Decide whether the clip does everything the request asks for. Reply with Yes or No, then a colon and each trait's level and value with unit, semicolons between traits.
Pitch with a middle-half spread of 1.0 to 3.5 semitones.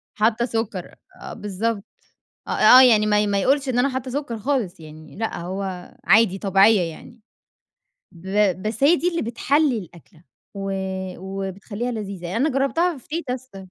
No: average, 4.9 semitones